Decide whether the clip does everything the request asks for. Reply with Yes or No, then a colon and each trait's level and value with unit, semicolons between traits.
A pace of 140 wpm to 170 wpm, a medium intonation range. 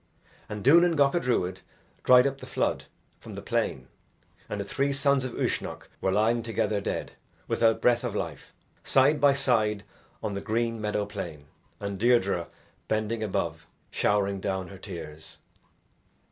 Yes: average, 150 wpm; average, 4.3 semitones